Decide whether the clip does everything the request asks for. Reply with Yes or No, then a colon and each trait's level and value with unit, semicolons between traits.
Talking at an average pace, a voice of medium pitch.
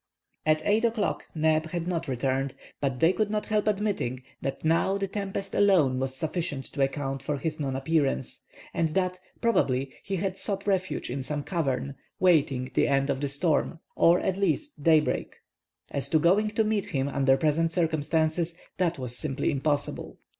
Yes: average, 175 wpm; medium, 160 Hz